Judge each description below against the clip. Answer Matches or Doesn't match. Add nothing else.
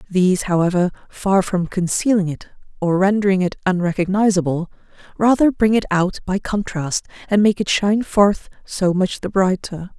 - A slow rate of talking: Doesn't match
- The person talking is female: Matches